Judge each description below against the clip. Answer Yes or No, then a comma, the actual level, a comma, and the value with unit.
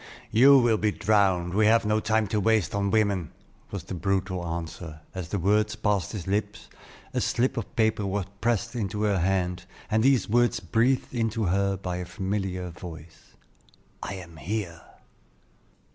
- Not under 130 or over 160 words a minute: No, average, 175 wpm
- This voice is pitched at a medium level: No, low, 100 Hz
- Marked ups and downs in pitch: No, average, 3.3 semitones